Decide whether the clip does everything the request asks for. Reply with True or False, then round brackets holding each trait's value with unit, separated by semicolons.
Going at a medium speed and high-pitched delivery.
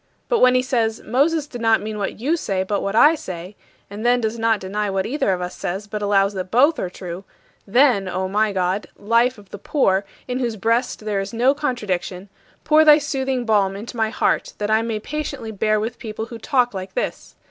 False (220 wpm; 220 Hz)